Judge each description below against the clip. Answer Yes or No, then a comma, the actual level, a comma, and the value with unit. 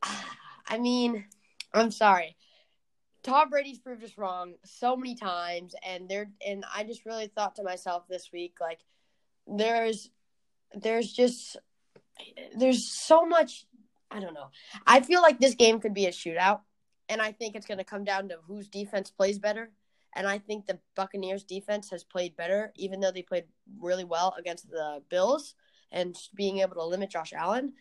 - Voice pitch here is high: Yes, high, 205 Hz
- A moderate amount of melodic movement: Yes, average, 3.8 semitones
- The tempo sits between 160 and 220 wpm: Yes, average, 175 wpm